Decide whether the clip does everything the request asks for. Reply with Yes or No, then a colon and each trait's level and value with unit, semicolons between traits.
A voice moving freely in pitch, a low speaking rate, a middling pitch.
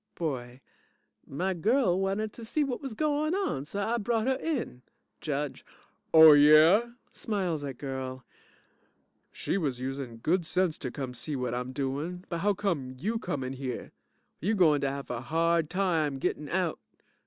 No: wide, 6.9 semitones; average, 165 wpm; medium, 160 Hz